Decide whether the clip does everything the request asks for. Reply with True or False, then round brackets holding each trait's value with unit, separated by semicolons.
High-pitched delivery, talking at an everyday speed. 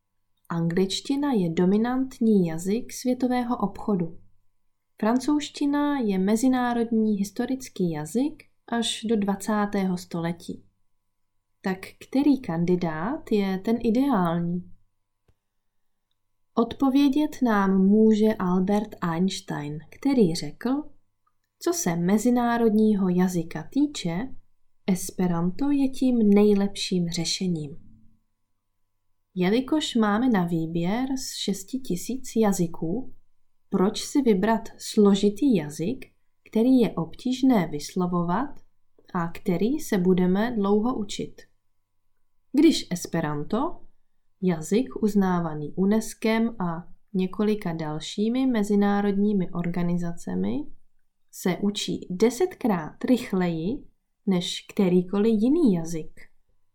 False (195 Hz; 85 wpm)